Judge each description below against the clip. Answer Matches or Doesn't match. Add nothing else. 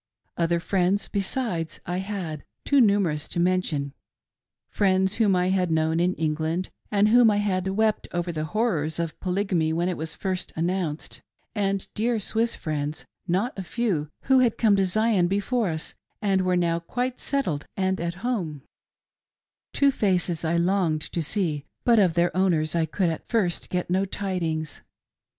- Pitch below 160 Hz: Doesn't match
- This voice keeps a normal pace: Matches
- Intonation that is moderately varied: Matches